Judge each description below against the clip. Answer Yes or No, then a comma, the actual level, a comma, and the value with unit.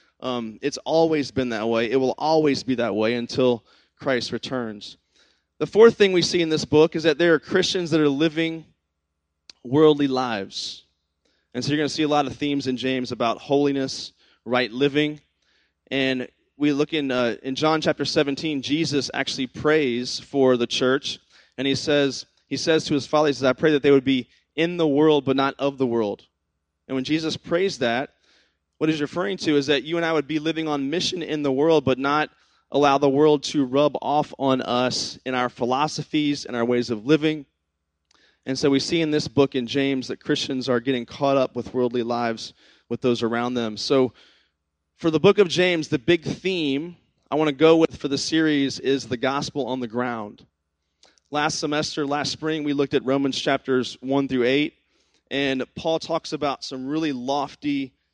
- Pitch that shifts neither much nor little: Yes, average, 3.6 semitones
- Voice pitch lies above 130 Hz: Yes, medium, 140 Hz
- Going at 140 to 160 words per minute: No, average, 195 wpm